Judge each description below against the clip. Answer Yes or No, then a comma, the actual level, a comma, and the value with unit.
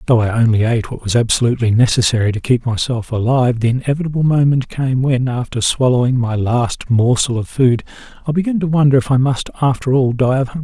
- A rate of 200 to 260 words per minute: Yes, fast, 205 wpm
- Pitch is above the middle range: No, low, 125 Hz